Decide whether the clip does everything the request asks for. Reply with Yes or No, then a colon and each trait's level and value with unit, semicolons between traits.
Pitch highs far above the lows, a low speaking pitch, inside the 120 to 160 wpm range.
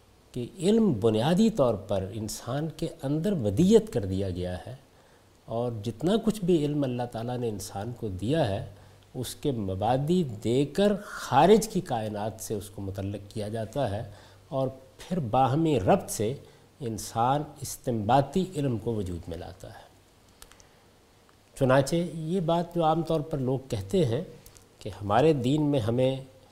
Yes: wide, 6.8 semitones; low, 125 Hz; average, 155 wpm